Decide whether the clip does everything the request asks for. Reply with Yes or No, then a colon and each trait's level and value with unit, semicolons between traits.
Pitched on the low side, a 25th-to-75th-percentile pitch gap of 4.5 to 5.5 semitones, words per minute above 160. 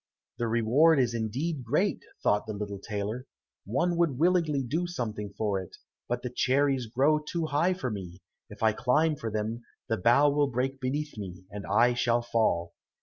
Yes: low, 120 Hz; average, 5.2 semitones; average, 180 wpm